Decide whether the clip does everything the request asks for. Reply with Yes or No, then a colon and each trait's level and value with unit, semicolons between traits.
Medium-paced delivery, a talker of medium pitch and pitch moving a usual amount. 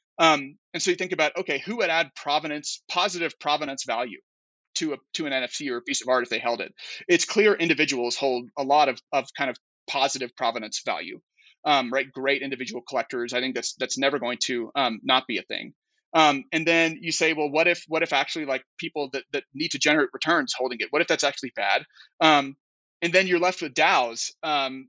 No: fast, 220 wpm; medium, 150 Hz; average, 4.1 semitones